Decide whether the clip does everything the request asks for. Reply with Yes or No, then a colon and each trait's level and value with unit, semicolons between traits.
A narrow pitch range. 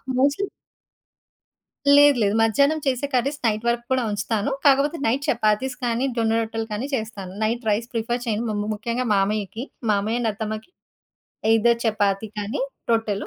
No: average, 3.0 semitones